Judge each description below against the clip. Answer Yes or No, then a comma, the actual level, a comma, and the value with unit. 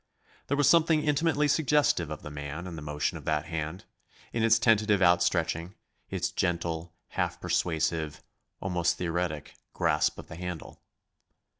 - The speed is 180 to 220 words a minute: No, average, 145 wpm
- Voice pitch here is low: Yes, very low, 85 Hz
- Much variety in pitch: Yes, wide, 5.7 semitones